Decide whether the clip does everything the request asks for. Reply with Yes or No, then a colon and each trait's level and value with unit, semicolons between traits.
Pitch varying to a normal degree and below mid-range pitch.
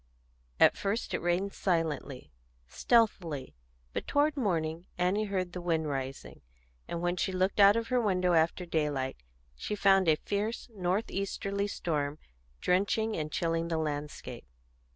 No: average, 4.0 semitones; medium, 180 Hz